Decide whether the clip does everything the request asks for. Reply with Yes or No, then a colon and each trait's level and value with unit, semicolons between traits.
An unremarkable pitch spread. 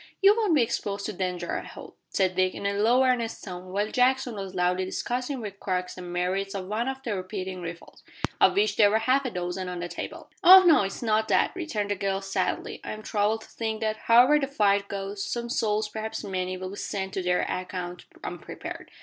Yes: average, 4.0 semitones